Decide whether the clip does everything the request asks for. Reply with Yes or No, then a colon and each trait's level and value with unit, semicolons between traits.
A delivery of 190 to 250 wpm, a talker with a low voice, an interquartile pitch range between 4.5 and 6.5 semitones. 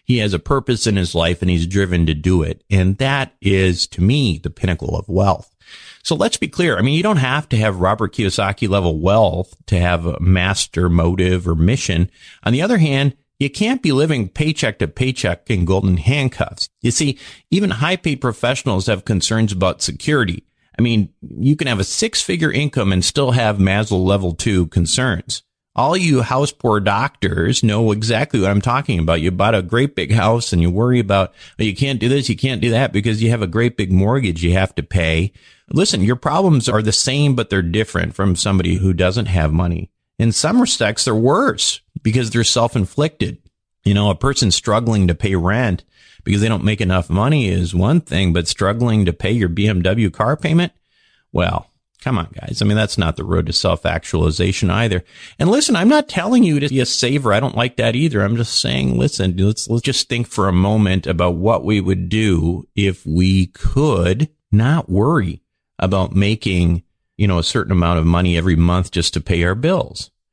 Yes: fast, 205 wpm; low, 105 Hz; wide, 5.4 semitones